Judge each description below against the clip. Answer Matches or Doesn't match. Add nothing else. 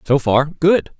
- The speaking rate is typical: Matches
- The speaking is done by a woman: Doesn't match